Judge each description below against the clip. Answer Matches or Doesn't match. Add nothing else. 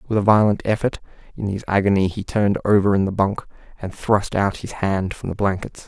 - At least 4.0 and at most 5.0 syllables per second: Doesn't match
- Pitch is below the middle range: Matches